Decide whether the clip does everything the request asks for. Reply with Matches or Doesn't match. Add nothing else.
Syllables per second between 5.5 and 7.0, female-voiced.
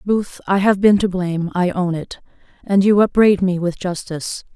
Doesn't match